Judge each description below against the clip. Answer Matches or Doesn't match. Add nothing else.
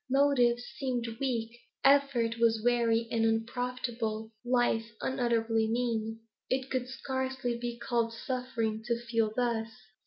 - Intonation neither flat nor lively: Doesn't match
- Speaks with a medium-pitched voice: Doesn't match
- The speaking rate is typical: Doesn't match